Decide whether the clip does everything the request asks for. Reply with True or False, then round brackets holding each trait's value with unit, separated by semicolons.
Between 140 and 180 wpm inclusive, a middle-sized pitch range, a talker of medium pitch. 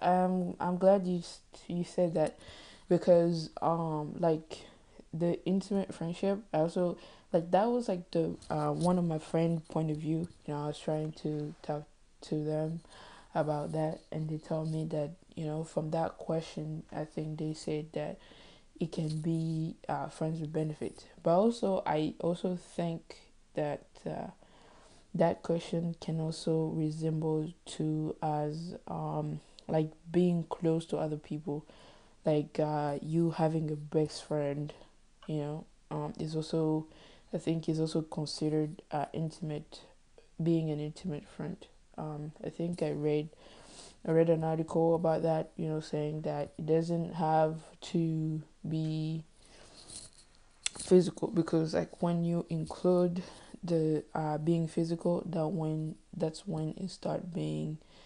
False (145 wpm; 1.6 semitones; 160 Hz)